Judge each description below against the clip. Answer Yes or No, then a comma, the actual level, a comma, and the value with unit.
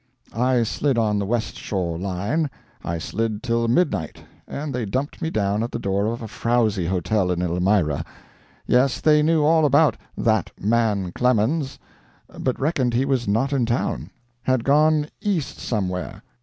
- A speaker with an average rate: Yes, average, 160 wpm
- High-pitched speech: No, low, 115 Hz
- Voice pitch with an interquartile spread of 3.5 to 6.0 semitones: Yes, wide, 5.5 semitones